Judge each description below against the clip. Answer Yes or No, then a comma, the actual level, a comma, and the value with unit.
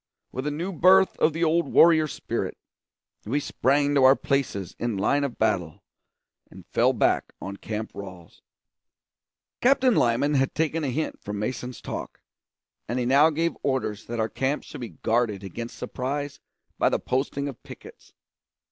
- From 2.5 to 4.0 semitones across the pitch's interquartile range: No, average, 4.8 semitones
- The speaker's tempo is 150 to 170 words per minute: Yes, average, 165 wpm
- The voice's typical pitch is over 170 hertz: No, low, 135 Hz